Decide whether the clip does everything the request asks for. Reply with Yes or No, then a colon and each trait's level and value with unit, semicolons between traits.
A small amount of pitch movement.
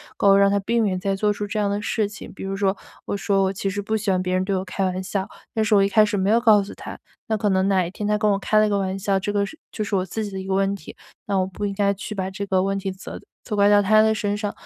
Yes: narrow, 1.4 semitones